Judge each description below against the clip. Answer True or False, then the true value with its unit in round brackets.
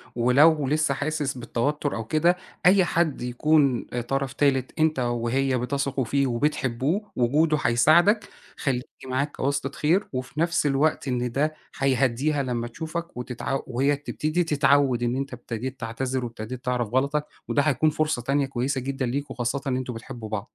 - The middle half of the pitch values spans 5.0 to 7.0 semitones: False (3.4 semitones)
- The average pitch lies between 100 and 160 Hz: True (135 Hz)